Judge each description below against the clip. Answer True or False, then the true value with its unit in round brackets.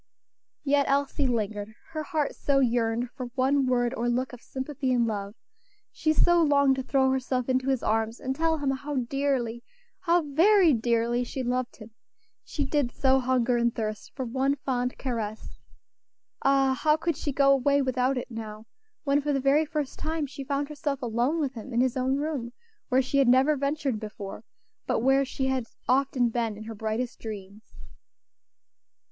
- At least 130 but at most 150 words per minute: False (180 wpm)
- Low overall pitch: False (260 Hz)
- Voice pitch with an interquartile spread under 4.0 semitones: True (2.9 semitones)